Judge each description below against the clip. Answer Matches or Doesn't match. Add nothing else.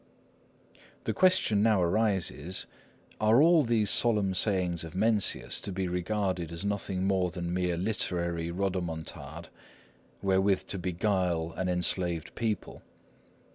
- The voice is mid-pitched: Doesn't match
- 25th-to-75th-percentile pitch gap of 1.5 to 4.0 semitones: Matches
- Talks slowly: Matches